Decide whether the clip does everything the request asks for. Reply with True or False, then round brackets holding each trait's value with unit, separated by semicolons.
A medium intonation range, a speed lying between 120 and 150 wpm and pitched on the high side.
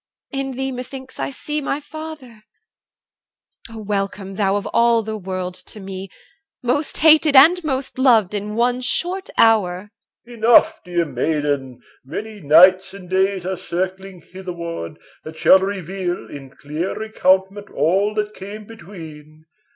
True (4.8 semitones; 145 wpm; 195 Hz)